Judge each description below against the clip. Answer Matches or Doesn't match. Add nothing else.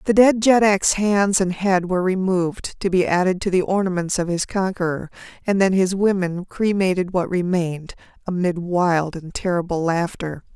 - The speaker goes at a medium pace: Matches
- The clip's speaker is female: Matches